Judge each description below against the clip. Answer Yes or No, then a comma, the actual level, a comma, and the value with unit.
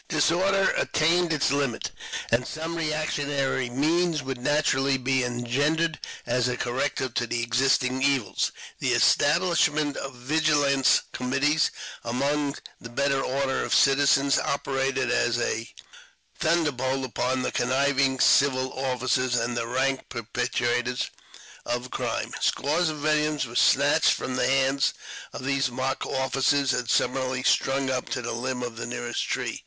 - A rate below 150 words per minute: Yes, average, 140 wpm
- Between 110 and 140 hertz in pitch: Yes, low, 135 Hz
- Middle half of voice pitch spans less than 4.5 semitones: Yes, narrow, 2.5 semitones